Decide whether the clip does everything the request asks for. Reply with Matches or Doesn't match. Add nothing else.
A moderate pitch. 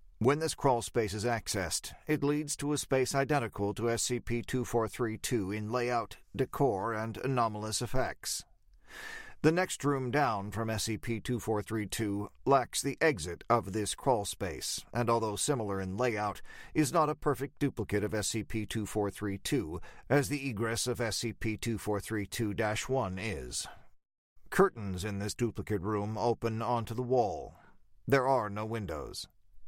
Doesn't match